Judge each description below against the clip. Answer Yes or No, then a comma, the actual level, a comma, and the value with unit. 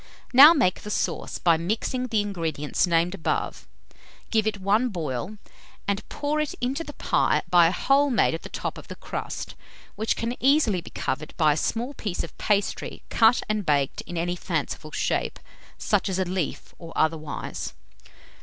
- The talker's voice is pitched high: Yes, high, 200 Hz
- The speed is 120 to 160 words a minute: No, average, 175 wpm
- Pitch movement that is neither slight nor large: No, wide, 6.2 semitones